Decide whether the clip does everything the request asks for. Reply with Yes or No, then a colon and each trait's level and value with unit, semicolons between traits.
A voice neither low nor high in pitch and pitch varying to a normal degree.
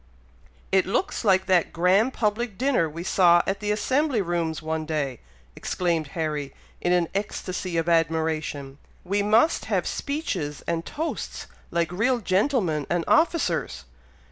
Yes: medium, 180 Hz; average, 4.5 semitones